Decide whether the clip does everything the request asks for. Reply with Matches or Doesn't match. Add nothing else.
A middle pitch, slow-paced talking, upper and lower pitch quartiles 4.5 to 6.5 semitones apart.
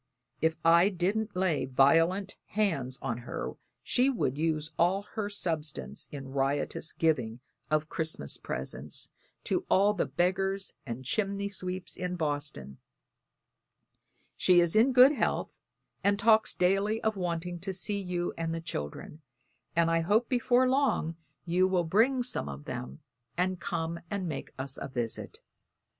Doesn't match